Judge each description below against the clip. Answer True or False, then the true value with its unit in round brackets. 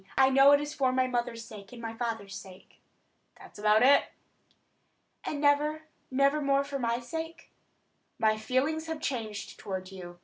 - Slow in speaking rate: False (165 wpm)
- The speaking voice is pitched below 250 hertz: False (255 Hz)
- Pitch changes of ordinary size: True (4.6 semitones)